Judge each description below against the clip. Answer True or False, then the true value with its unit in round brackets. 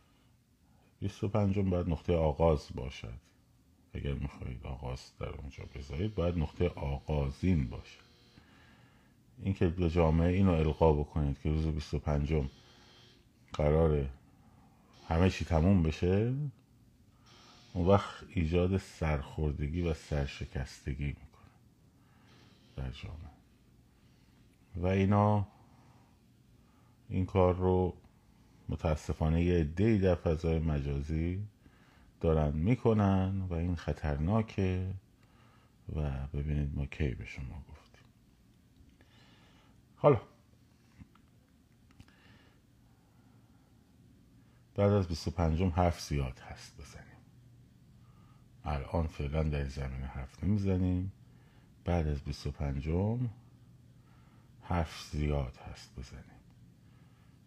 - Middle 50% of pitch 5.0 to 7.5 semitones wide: True (5.4 semitones)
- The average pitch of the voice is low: True (85 Hz)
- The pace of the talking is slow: True (90 wpm)